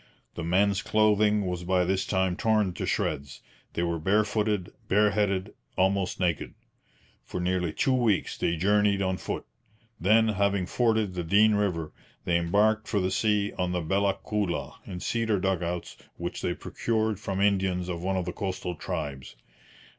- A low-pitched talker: Yes, very low, 95 Hz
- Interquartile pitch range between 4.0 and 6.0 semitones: No, average, 2.8 semitones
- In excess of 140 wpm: Yes, average, 160 wpm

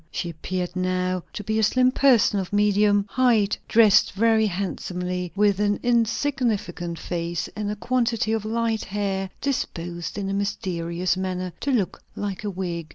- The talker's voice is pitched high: Yes, high, 200 Hz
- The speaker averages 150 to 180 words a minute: Yes, average, 160 wpm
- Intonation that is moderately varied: Yes, average, 3.3 semitones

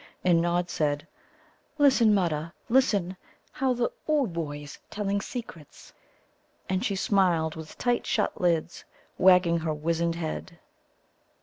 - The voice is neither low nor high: Yes, medium, 175 Hz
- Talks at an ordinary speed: No, slow, 115 wpm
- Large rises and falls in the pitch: No, average, 4.2 semitones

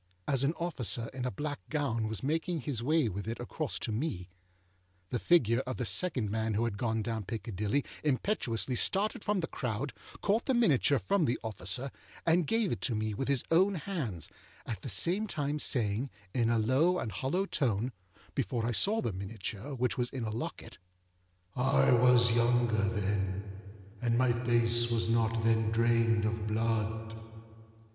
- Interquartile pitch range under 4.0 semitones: No, average, 4.3 semitones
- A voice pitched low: Yes, low, 120 Hz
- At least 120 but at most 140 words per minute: No, average, 170 wpm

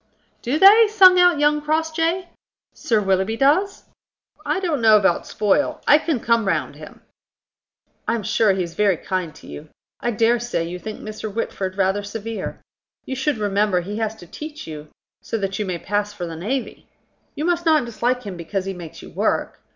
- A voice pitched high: Yes, high, 220 Hz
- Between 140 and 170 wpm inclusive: No, average, 190 wpm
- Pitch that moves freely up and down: Yes, wide, 7.4 semitones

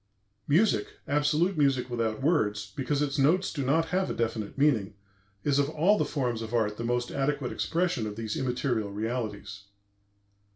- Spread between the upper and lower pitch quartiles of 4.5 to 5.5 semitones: Yes, average, 5.1 semitones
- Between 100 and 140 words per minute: No, average, 165 wpm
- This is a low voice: Yes, low, 130 Hz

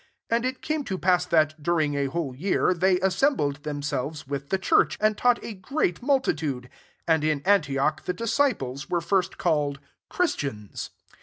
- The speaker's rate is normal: Yes, average, 170 wpm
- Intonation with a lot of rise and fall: Yes, wide, 5.9 semitones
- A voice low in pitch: No, medium, 170 Hz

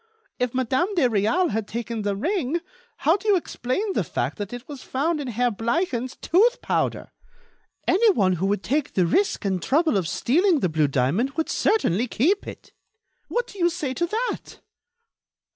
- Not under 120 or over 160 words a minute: No, average, 175 wpm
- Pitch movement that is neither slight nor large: No, wide, 8.5 semitones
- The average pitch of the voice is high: Yes, very high, 260 Hz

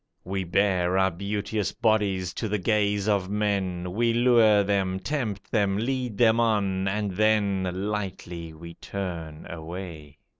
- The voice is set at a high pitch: No, low, 100 Hz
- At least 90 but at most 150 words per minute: Yes, average, 140 wpm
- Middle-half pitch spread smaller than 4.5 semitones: Yes, narrow, 2.5 semitones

